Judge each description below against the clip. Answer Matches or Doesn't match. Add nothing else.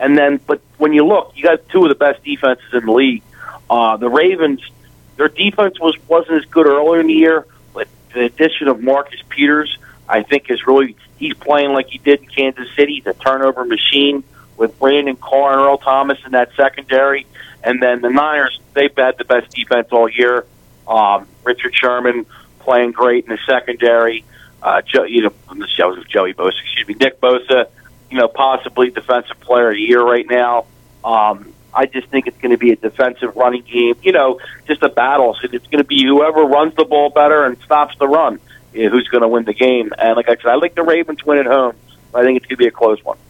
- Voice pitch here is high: Doesn't match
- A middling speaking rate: Doesn't match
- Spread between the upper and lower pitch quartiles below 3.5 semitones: Matches